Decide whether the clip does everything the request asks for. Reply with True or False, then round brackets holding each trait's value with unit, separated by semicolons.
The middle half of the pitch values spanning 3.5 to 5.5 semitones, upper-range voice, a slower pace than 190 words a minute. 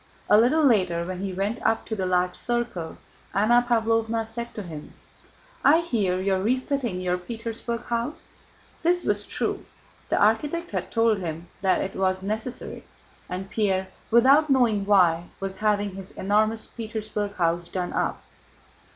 True (3.9 semitones; 210 Hz; 155 wpm)